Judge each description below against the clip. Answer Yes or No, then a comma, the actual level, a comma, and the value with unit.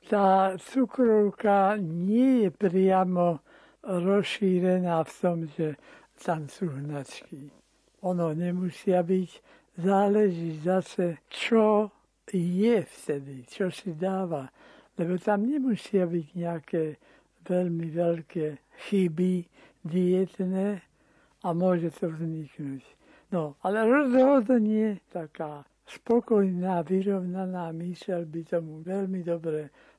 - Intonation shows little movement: No, average, 3.0 semitones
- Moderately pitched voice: Yes, medium, 180 Hz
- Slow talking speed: Yes, slow, 95 wpm